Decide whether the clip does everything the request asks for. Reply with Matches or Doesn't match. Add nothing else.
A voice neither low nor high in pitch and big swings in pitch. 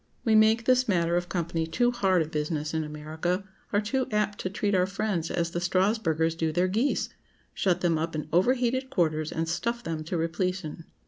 Doesn't match